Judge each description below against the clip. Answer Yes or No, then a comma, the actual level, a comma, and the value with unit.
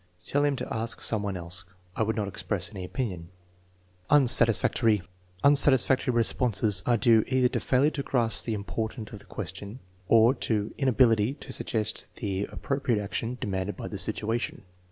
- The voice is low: Yes, low, 115 Hz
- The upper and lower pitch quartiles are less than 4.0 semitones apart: Yes, average, 3.6 semitones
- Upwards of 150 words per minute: Yes, average, 160 wpm